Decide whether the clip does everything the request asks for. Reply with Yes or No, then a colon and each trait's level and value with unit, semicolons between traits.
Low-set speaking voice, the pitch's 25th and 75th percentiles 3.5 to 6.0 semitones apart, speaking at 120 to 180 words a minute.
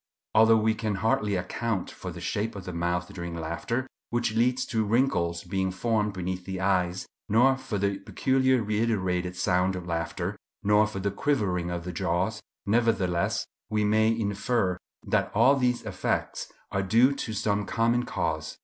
Yes: low, 100 Hz; average, 3.9 semitones; average, 165 wpm